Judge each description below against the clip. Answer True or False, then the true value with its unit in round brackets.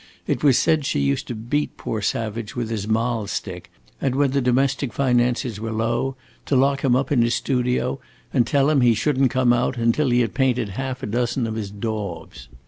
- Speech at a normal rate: False (215 wpm)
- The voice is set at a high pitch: False (125 Hz)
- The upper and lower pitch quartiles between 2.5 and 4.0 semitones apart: True (3.0 semitones)